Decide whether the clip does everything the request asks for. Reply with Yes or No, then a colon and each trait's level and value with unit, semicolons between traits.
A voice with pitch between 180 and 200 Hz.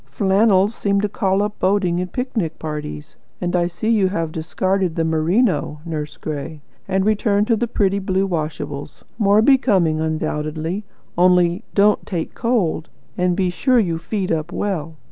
Yes: medium, 185 Hz